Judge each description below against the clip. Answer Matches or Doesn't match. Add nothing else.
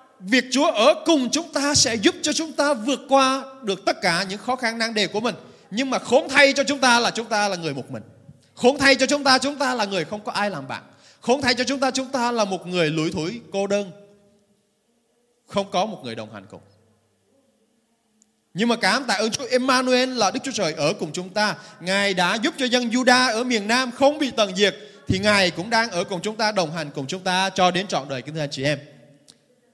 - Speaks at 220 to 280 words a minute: Matches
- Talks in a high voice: Matches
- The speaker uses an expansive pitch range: Matches